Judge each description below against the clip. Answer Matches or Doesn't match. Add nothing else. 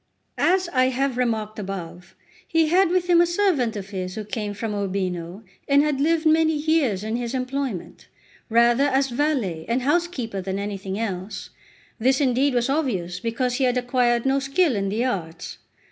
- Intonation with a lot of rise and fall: Matches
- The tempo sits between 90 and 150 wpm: Doesn't match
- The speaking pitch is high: Matches